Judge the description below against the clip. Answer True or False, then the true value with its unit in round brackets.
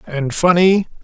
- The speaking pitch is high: False (170 Hz)